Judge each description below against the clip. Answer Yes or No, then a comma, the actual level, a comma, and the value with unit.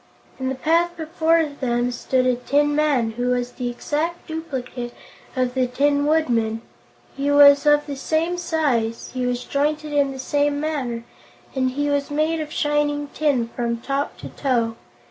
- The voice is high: Yes, very high, 285 Hz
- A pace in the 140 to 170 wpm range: Yes, average, 165 wpm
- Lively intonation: No, average, 3.3 semitones